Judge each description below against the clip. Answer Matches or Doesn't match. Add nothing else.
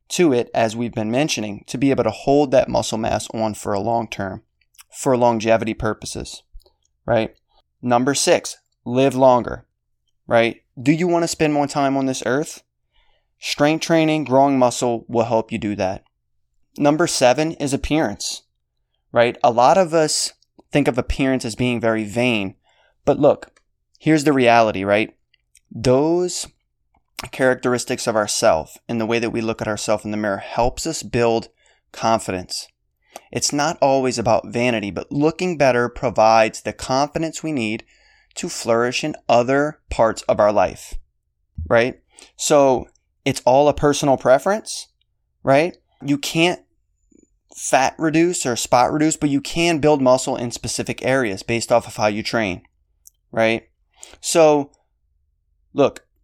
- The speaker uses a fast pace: Doesn't match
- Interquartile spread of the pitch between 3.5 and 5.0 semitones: Matches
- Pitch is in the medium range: Doesn't match